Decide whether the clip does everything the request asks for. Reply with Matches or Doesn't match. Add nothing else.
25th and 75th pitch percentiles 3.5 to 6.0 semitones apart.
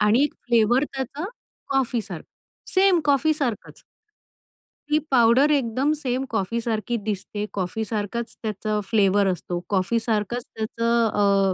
Matches